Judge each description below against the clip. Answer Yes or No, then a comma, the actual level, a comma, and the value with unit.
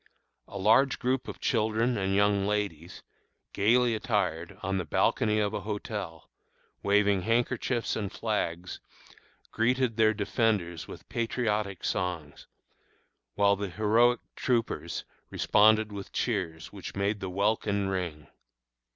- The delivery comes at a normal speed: No, slow, 120 wpm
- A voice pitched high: No, low, 105 Hz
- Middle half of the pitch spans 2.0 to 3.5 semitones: Yes, average, 2.7 semitones